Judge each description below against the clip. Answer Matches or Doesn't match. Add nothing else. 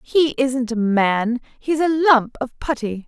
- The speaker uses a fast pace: Doesn't match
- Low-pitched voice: Doesn't match